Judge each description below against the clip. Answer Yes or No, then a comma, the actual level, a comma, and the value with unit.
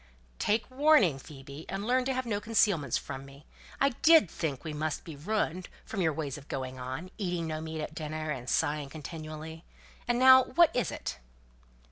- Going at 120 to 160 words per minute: No, average, 185 wpm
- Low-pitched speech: No, medium, 160 Hz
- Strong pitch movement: Yes, wide, 6.8 semitones